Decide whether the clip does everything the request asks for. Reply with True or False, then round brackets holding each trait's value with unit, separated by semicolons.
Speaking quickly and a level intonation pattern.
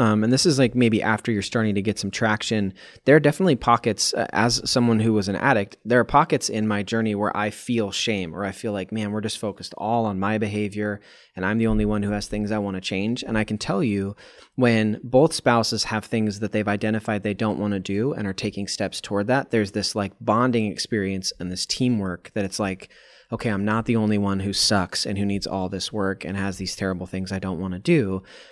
True (245 wpm; 2.3 semitones)